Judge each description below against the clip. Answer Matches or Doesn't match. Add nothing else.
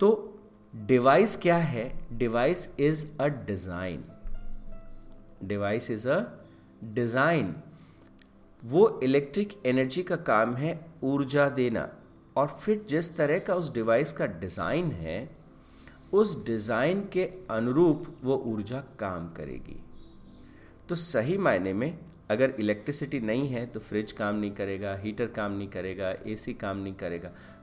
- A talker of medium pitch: Doesn't match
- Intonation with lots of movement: Matches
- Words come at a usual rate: Matches